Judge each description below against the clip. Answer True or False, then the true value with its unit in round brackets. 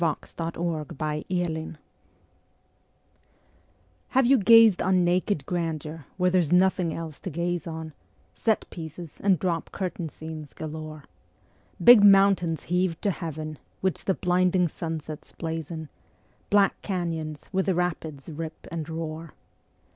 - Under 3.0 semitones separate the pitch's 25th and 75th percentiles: True (2.6 semitones)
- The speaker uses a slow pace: True (130 wpm)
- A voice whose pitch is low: False (170 Hz)